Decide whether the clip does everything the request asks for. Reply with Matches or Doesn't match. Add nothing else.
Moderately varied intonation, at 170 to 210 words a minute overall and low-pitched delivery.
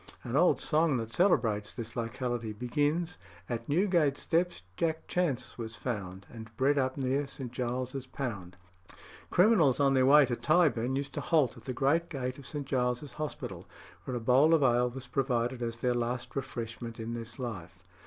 Matches